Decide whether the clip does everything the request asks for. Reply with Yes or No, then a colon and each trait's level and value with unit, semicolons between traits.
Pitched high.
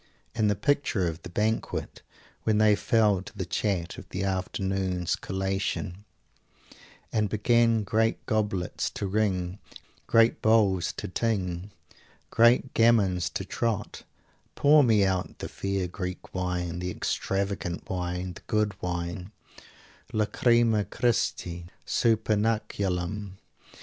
No: low, 100 Hz